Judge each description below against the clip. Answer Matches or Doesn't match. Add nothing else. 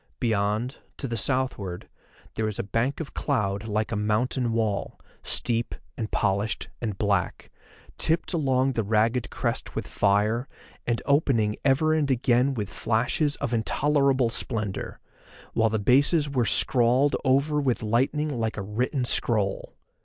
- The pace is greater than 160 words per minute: Doesn't match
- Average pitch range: Matches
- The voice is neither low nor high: Doesn't match